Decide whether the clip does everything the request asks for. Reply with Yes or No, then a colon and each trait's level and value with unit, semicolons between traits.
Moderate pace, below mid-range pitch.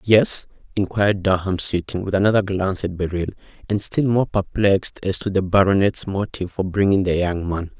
Yes: average, 175 wpm; very low, 95 Hz